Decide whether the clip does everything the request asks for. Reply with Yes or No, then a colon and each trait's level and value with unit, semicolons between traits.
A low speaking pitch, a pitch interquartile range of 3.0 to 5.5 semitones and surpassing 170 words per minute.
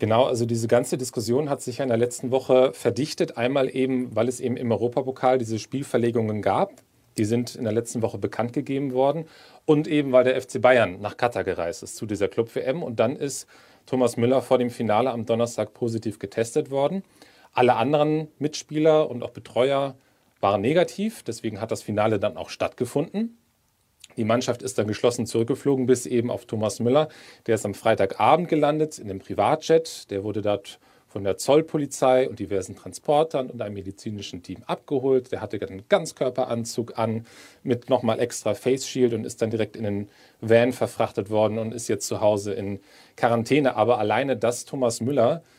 Yes: low, 125 Hz; average, 3.3 semitones; average, 180 wpm